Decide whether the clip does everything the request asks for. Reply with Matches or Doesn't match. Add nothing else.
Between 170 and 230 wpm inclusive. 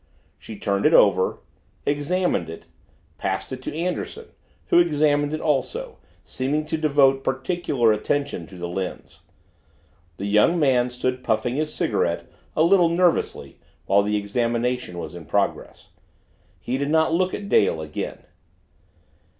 Doesn't match